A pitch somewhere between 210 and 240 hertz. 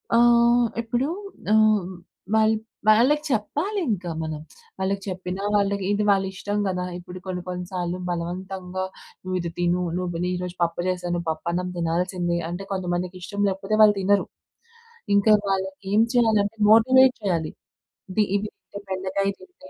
No: high, 190 Hz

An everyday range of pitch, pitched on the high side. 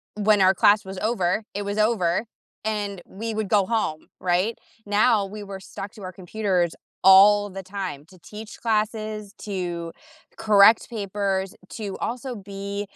No: narrow, 2.1 semitones; high, 200 Hz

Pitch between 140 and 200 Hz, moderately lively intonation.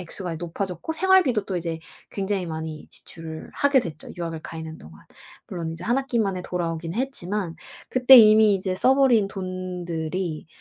Yes: medium, 185 Hz; average, 4.8 semitones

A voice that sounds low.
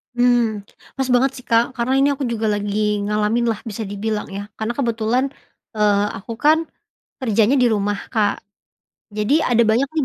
No: high, 225 Hz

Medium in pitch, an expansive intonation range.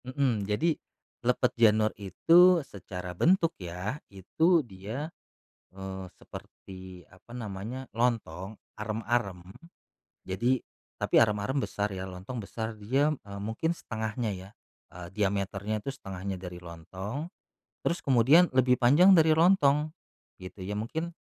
No: low, 110 Hz; wide, 5.7 semitones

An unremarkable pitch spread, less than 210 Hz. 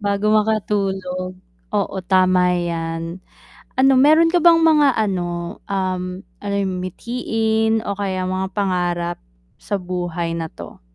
Yes: average, 3.3 semitones; high, 190 Hz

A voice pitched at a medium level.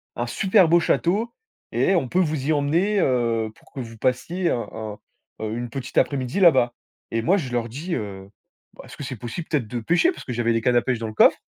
No: low, 130 Hz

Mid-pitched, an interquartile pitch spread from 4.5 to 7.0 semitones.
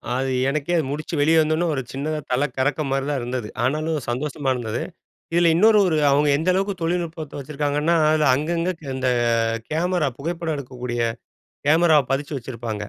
No: medium, 150 Hz; average, 3.5 semitones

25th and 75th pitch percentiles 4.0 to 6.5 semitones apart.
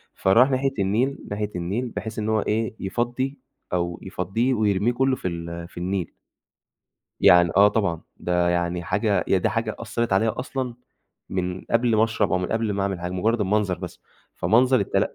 Yes: average, 4.4 semitones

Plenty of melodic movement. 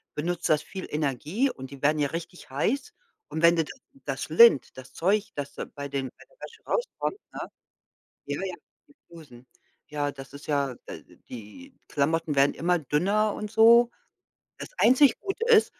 Yes: wide, 7.1 semitones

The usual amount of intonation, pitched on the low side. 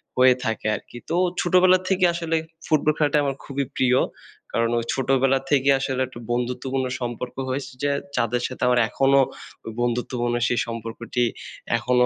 No: narrow, 2.3 semitones; low, 130 Hz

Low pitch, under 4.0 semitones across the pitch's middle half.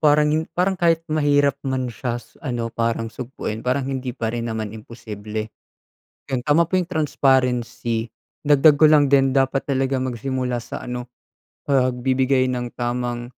Yes: low, 130 Hz; average, 2.9 semitones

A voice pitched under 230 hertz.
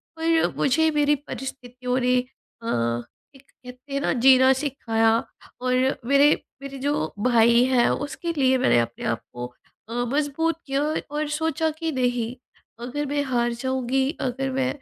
No: very high, 265 Hz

